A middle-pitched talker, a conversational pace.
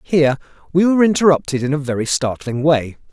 Yes: medium, 150 Hz; average, 175 wpm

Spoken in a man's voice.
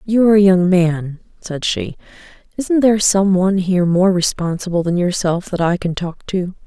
No: female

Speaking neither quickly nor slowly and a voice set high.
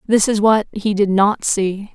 No: fast, 215 wpm; high, 205 Hz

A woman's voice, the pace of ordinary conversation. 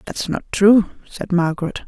Yes: female; average, 160 wpm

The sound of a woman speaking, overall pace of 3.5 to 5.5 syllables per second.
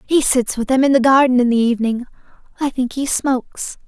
No: female; 5.8 syllables/s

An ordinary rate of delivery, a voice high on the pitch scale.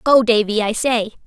Yes: average, 190 wpm; high, 225 Hz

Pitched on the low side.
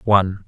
Yes: very low, 95 Hz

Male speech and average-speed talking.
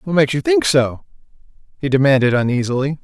Yes: male; average, 160 wpm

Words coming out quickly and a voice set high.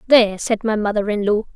Yes: fast, 230 wpm; high, 215 Hz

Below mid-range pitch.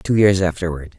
Yes: very low, 90 Hz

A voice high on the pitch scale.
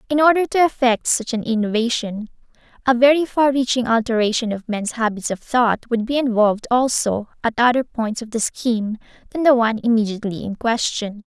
Yes: high, 235 Hz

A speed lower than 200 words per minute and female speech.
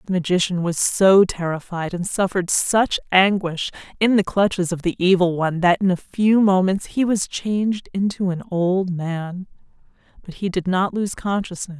Yes: average, 175 wpm; female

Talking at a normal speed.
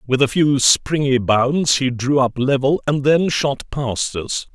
Yes: average, 185 wpm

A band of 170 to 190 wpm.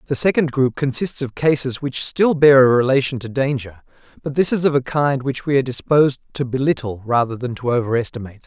No: fast, 205 wpm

